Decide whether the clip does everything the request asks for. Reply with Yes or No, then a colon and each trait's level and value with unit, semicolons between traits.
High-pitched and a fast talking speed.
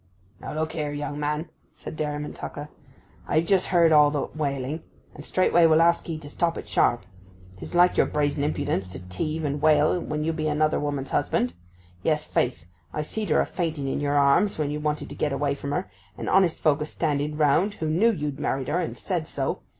No: medium, 150 Hz; fast, 210 wpm